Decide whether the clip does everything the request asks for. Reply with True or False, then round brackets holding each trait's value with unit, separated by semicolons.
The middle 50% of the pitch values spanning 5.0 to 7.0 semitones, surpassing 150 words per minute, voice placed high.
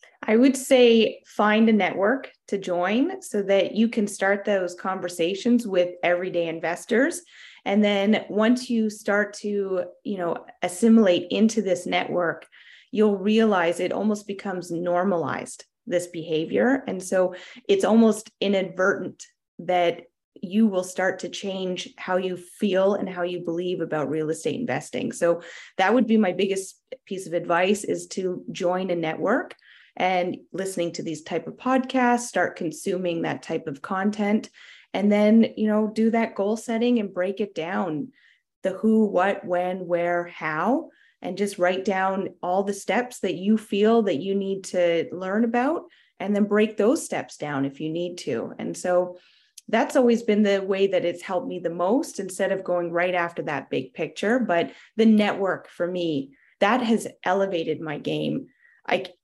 False (3.5 semitones; 165 wpm; 195 Hz)